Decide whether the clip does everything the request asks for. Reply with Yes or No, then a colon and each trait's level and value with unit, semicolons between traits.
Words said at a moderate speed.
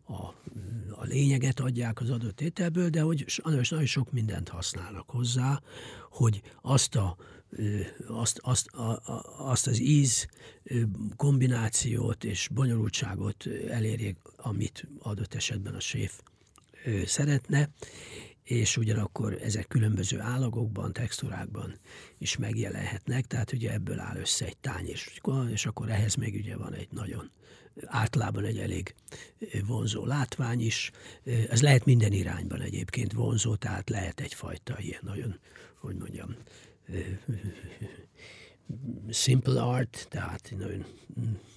No: slow, 115 wpm